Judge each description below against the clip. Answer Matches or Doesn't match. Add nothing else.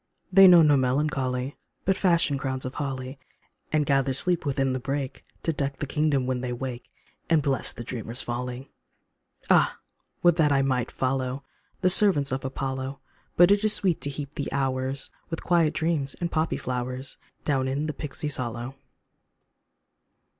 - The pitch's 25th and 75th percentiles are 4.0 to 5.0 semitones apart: Doesn't match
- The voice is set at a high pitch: Doesn't match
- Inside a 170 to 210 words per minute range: Matches